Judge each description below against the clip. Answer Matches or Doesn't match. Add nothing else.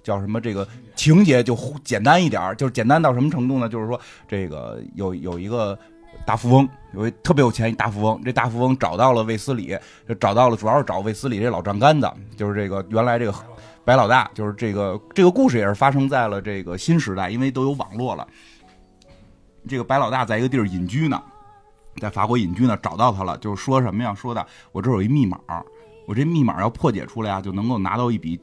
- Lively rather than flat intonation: Doesn't match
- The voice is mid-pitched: Doesn't match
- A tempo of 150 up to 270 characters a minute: Doesn't match